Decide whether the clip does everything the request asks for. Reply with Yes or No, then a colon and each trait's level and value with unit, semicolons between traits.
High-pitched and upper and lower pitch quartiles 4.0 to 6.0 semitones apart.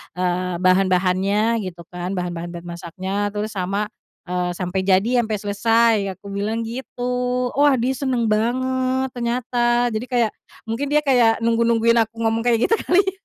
Yes: high, 225 Hz; average, 4.3 semitones